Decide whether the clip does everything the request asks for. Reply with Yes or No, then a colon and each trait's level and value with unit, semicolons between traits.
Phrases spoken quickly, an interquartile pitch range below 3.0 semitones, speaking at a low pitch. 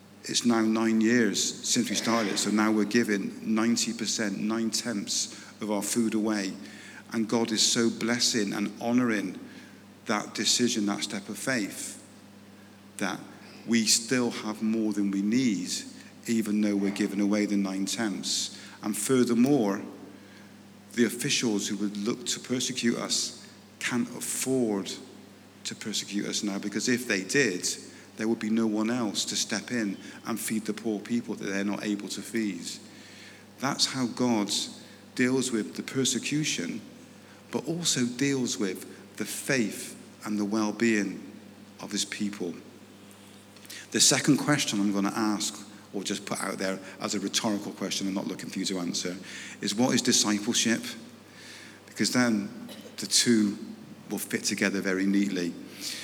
No: average, 155 wpm; narrow, 2.6 semitones; low, 105 Hz